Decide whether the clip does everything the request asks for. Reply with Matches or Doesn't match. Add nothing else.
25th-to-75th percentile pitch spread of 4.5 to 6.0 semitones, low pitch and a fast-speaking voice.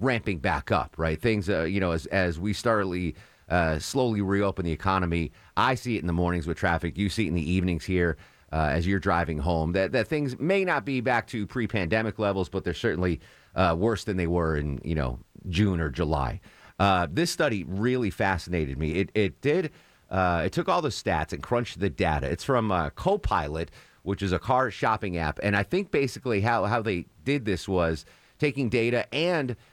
Matches